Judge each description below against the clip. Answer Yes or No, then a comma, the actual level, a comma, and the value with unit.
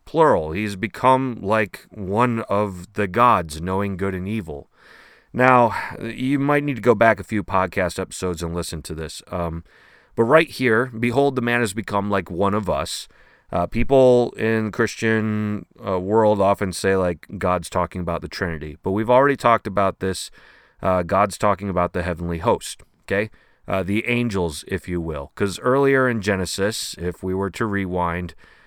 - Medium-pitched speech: No, low, 100 Hz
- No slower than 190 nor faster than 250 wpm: No, average, 175 wpm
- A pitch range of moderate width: Yes, average, 4.3 semitones